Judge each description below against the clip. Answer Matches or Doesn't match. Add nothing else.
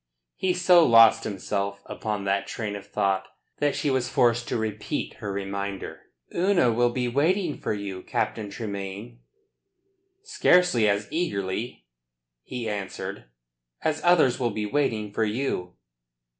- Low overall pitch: Matches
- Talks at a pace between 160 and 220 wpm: Doesn't match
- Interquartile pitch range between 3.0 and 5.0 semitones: Doesn't match